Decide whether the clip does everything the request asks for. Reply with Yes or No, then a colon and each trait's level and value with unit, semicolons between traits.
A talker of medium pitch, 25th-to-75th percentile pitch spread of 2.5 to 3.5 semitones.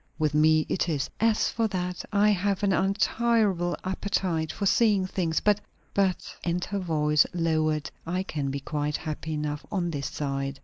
No: medium, 175 Hz; average, 4.6 semitones